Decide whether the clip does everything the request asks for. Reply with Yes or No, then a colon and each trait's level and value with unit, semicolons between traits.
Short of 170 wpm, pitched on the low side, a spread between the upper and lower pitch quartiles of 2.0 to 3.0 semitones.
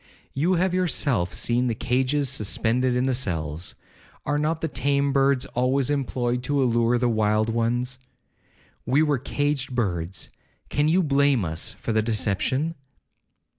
No: average, 140 wpm; low, 125 Hz; average, 3.7 semitones